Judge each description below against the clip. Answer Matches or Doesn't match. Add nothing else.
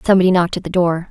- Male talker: Doesn't match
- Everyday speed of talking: Doesn't match